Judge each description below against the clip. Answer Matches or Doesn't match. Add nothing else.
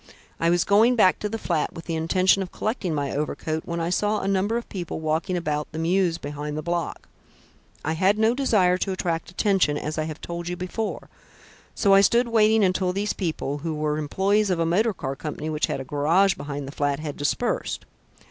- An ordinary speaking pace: Doesn't match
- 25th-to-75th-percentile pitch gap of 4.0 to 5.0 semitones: Matches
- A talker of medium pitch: Matches